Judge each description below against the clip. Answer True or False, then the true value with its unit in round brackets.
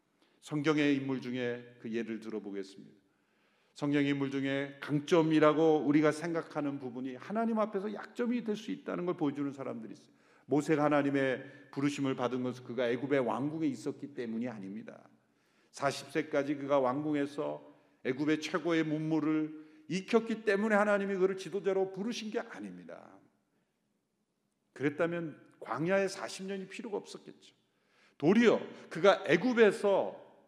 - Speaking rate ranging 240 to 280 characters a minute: False (325 characters per minute)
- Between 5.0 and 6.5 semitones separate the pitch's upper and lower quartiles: True (5.5 semitones)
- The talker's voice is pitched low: False (150 Hz)